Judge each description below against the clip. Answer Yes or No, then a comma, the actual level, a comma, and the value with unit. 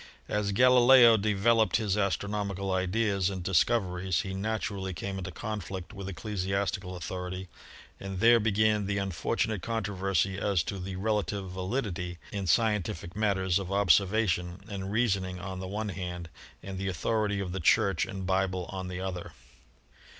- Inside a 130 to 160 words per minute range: Yes, average, 150 wpm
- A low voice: Yes, very low, 95 Hz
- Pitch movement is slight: Yes, narrow, 2.2 semitones